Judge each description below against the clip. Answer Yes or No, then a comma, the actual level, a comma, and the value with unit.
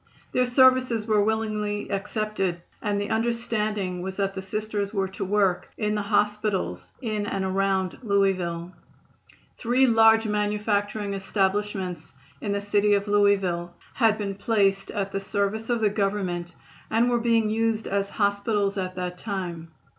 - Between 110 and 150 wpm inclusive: Yes, average, 145 wpm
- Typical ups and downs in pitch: No, narrow, 2.0 semitones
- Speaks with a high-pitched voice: Yes, high, 205 Hz